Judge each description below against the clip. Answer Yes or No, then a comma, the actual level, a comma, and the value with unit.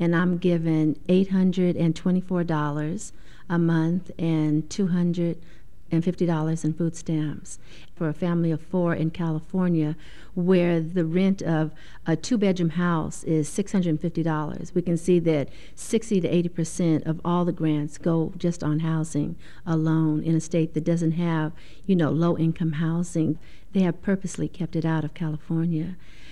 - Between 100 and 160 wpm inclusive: Yes, average, 140 wpm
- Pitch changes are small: Yes, narrow, 1.9 semitones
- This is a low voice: No, medium, 165 Hz